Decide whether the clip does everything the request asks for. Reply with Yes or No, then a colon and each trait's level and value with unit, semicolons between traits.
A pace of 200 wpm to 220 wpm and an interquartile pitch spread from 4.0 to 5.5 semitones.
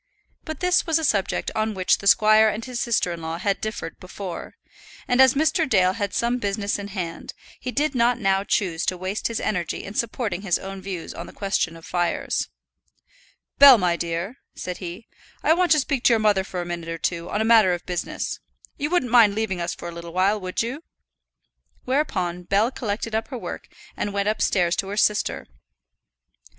Yes: fast, 205 wpm; average, 4.6 semitones